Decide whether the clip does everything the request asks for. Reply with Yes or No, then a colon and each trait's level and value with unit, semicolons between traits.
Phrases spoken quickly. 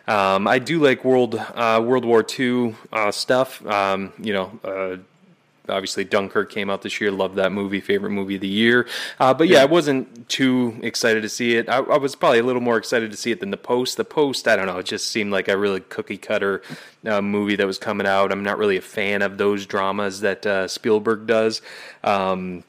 Yes: fast, 225 wpm